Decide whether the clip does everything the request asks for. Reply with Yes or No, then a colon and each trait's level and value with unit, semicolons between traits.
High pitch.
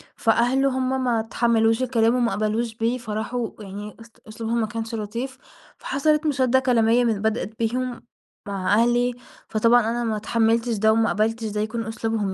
Yes: high, 230 Hz